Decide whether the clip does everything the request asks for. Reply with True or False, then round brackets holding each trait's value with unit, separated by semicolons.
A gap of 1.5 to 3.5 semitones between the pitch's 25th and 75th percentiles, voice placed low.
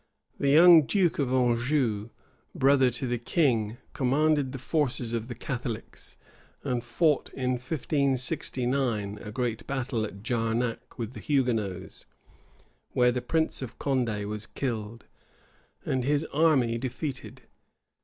True (3.1 semitones; 125 Hz)